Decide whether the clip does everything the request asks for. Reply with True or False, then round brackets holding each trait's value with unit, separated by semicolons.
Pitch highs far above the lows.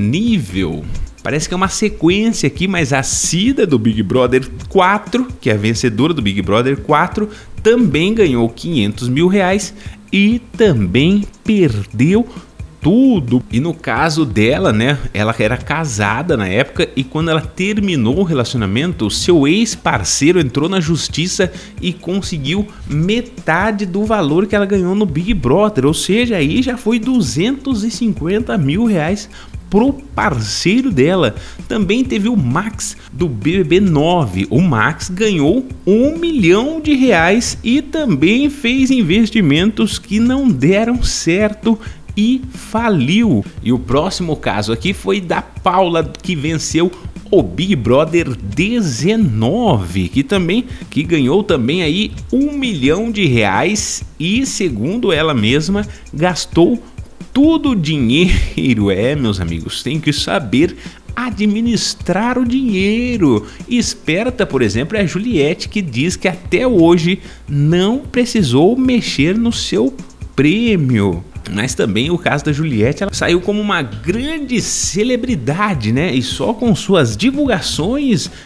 True (7.9 semitones)